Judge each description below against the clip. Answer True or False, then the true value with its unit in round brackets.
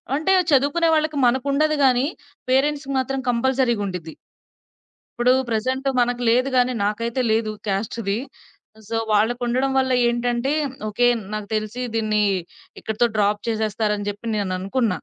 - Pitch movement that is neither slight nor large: True (3.7 semitones)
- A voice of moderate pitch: False (240 Hz)